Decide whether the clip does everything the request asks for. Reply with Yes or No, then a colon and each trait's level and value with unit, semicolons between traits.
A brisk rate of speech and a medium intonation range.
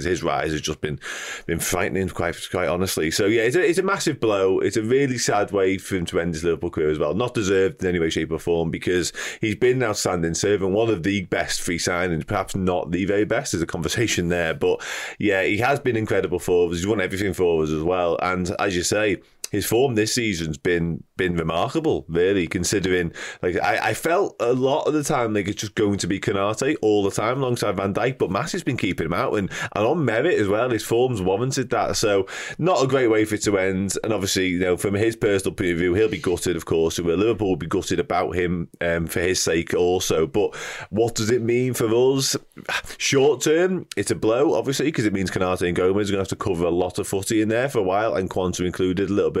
Yes: fast, 250 wpm; average, 4.3 semitones